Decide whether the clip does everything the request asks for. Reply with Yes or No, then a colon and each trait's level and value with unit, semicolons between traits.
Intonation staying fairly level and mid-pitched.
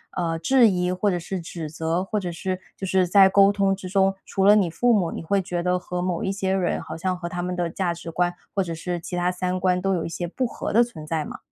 Yes: narrow, 2.0 semitones; medium, 180 Hz